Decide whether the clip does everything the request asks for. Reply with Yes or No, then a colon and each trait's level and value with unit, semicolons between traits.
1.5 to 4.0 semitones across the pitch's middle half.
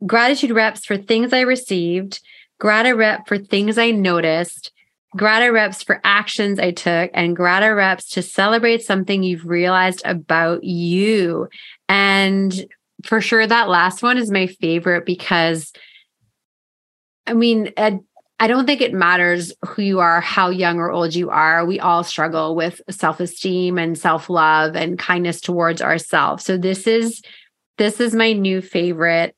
Yes: average, 3.7 semitones